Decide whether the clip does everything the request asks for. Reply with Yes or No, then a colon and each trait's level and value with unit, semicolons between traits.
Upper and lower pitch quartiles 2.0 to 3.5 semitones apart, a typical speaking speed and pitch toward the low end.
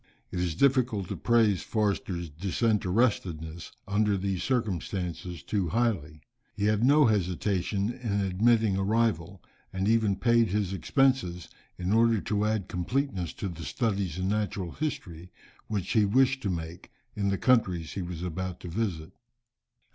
No: average, 3.9 semitones; average, 145 wpm; low, 100 Hz